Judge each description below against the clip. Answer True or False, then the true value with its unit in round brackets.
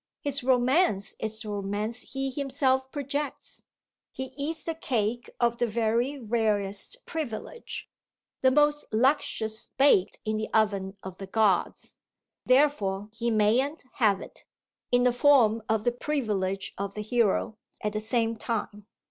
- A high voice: True (230 Hz)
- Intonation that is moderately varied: True (4.0 semitones)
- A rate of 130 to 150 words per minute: True (140 wpm)